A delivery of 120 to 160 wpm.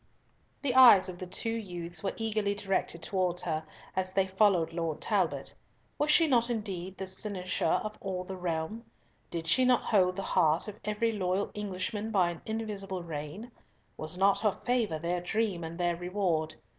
No: average, 175 wpm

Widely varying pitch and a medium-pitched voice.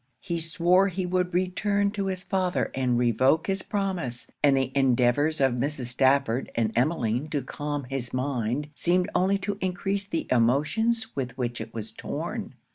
Yes: wide, 6.6 semitones; medium, 150 Hz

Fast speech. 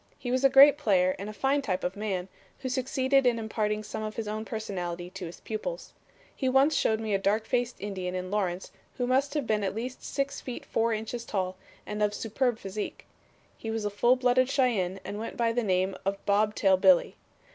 Yes: fast, 215 wpm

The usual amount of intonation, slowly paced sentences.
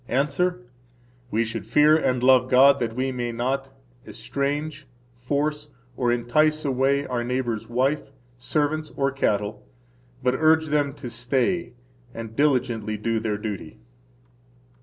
Yes: average, 3.6 semitones; slow, 130 wpm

